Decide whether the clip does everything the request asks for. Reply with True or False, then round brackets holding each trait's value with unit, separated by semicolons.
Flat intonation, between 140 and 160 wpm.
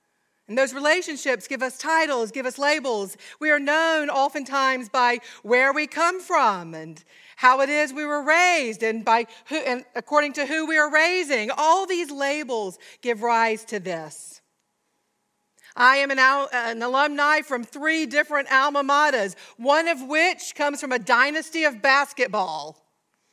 False (3.6 semitones; 155 wpm)